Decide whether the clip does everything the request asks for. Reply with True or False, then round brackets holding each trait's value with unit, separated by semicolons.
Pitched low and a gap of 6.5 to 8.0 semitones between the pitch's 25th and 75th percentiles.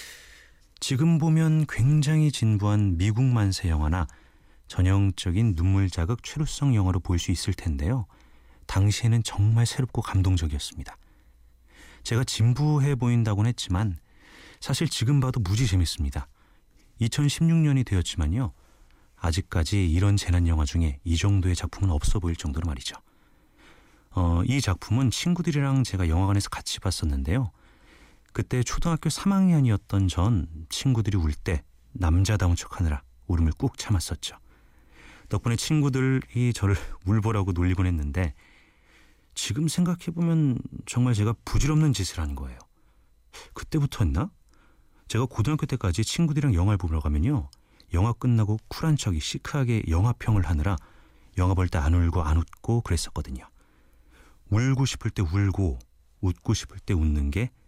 True (100 Hz; 6.9 semitones)